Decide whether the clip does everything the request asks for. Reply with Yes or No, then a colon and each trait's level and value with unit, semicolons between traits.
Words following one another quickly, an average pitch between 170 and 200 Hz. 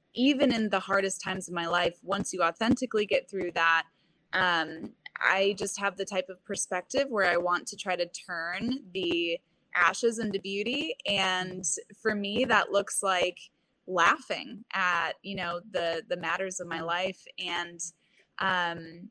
No: average, 160 wpm; medium, 185 Hz